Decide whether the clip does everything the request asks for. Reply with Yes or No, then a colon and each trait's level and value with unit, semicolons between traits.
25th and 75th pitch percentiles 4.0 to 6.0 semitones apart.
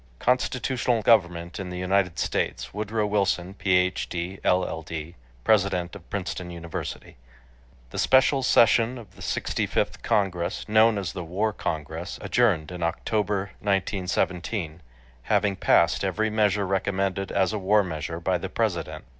No: average, 3.2 semitones